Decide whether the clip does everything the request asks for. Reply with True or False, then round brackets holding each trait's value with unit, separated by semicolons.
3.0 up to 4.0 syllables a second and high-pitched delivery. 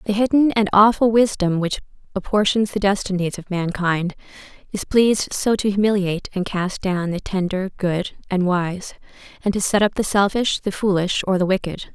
False (5.0 syllables/s; 195 Hz)